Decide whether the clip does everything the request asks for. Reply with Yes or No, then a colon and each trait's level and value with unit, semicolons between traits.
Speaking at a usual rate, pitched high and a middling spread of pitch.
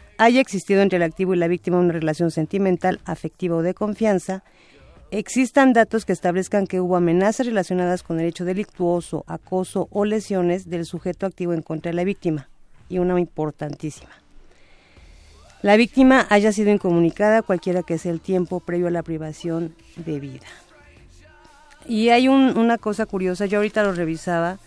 No: average, 165 wpm; medium, 180 Hz; average, 3.6 semitones